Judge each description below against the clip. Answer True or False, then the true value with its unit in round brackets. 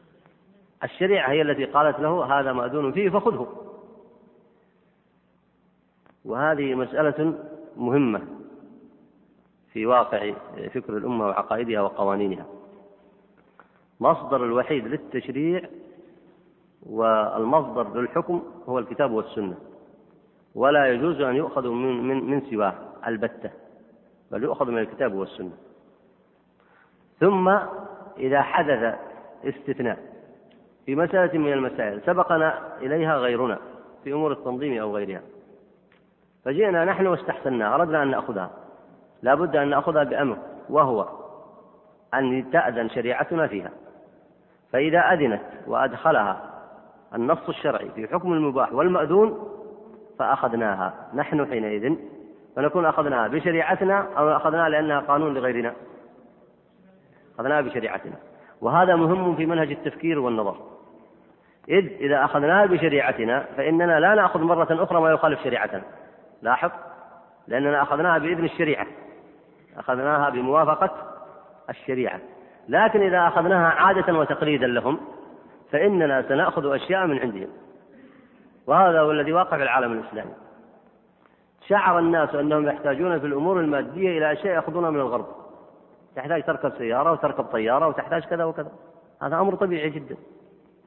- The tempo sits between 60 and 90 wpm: False (105 wpm)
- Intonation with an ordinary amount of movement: True (4.7 semitones)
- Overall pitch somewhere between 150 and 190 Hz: True (155 Hz)